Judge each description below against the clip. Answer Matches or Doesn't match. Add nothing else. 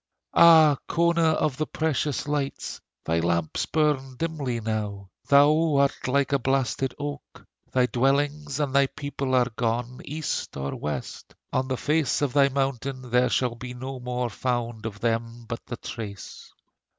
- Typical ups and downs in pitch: Matches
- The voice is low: Matches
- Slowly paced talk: Doesn't match